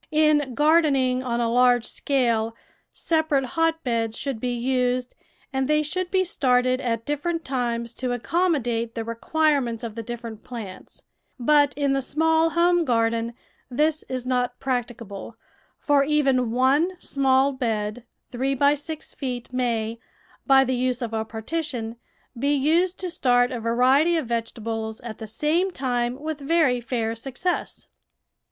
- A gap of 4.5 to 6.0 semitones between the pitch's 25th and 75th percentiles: No, average, 4.1 semitones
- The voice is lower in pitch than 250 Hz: No, very high, 255 Hz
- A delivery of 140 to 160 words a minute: Yes, average, 145 wpm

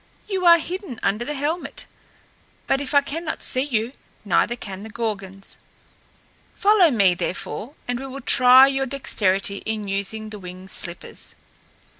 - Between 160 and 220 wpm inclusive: No, average, 150 wpm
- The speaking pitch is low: No, high, 240 Hz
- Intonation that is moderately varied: No, wide, 6.0 semitones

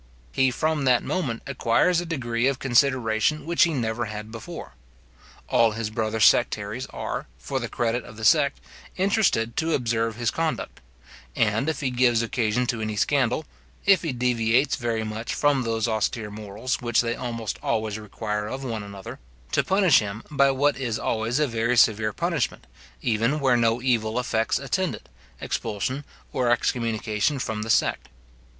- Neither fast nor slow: Yes, average, 165 wpm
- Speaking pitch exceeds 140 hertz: No, low, 120 Hz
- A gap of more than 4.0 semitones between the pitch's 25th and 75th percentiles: No, average, 3.6 semitones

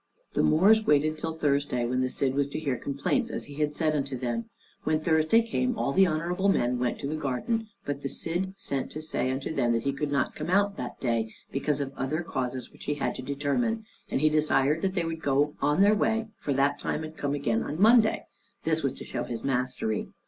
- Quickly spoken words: Yes, fast, 230 wpm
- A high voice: No, medium, 145 Hz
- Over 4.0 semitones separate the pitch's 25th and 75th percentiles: No, average, 3.7 semitones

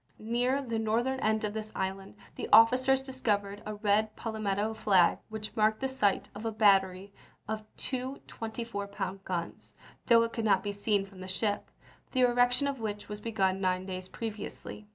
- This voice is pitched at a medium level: No, high, 215 Hz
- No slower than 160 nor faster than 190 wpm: Yes, average, 175 wpm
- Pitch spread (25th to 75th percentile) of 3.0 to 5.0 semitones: No, narrow, 2.5 semitones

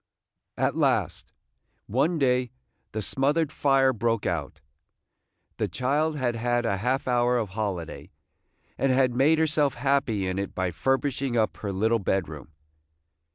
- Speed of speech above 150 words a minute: No, average, 140 wpm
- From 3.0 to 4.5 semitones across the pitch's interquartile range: No, average, 5.1 semitones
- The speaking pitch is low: Yes, low, 120 Hz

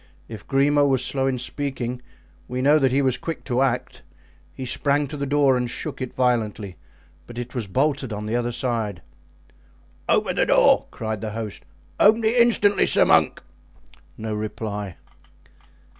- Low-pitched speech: Yes, low, 125 Hz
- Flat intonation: No, average, 4.0 semitones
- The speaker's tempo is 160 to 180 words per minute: Yes, average, 165 wpm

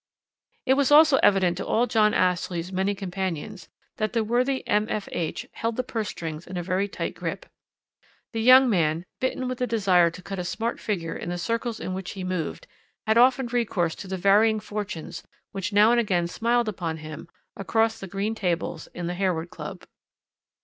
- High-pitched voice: Yes, high, 200 Hz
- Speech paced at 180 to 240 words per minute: Yes, average, 185 wpm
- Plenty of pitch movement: No, average, 4.4 semitones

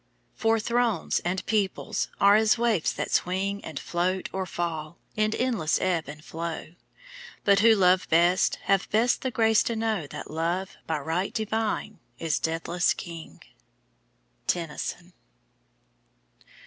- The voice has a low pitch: No, medium, 185 Hz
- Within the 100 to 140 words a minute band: Yes, slow, 135 wpm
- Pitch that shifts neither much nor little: Yes, average, 4.6 semitones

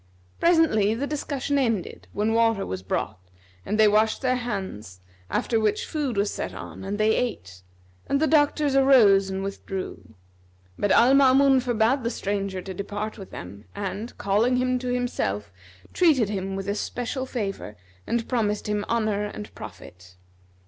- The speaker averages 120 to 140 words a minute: No, average, 155 wpm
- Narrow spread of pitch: No, average, 4.4 semitones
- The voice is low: No, high, 215 Hz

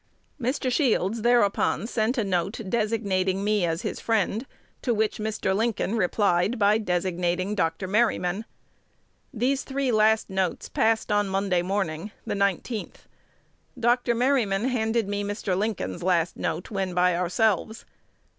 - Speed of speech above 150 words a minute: No, slow, 135 wpm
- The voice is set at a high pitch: Yes, high, 205 Hz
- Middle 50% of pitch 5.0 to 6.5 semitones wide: No, average, 3.4 semitones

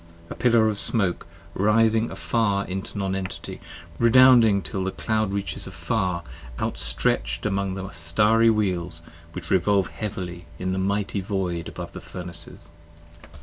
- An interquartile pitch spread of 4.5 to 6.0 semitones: No, average, 2.8 semitones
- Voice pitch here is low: Yes, low, 100 Hz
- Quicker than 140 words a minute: No, slow, 135 wpm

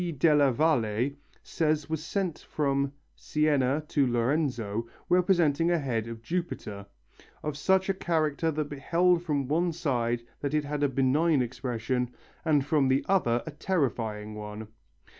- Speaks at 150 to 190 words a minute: No, average, 140 wpm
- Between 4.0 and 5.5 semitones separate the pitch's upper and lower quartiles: Yes, average, 4.6 semitones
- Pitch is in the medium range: Yes, medium, 145 Hz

